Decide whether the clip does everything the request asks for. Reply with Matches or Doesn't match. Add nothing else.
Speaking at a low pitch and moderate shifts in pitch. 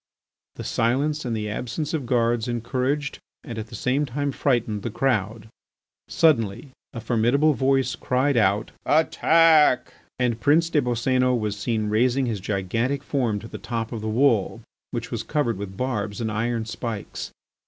Matches